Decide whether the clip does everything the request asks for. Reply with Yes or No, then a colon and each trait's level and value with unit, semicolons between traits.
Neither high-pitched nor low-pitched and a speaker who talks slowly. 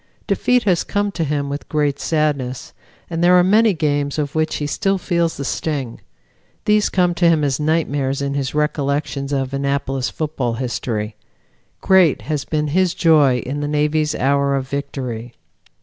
No: medium, 145 Hz; average, 165 wpm